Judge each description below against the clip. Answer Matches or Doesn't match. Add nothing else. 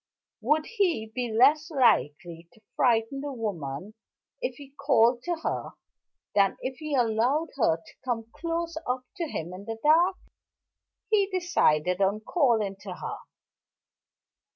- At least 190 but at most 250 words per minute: Doesn't match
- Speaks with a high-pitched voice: Matches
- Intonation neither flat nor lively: Doesn't match